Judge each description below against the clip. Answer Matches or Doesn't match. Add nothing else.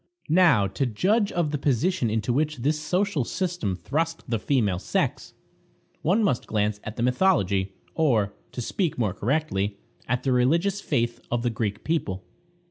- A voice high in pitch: Doesn't match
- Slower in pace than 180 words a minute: Matches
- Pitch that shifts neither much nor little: Doesn't match